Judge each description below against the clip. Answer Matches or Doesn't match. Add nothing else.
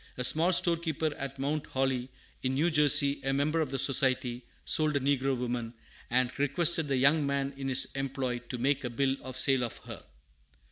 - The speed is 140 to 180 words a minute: Doesn't match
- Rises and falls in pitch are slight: Matches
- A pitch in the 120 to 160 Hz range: Matches